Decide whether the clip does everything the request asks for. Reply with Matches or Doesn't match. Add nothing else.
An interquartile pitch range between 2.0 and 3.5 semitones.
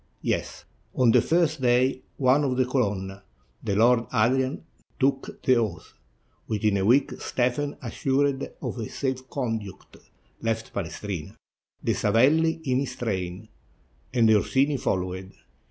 Doesn't match